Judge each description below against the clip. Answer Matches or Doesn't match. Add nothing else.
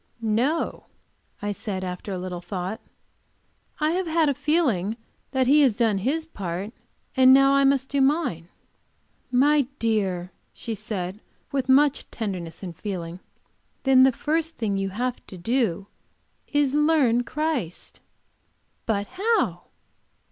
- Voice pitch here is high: Matches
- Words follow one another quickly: Doesn't match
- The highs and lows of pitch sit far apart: Matches